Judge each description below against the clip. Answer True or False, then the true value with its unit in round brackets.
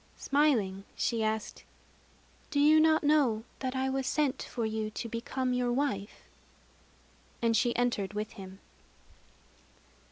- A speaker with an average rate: False (125 wpm)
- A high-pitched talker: True (245 Hz)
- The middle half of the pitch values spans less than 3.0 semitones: False (4.0 semitones)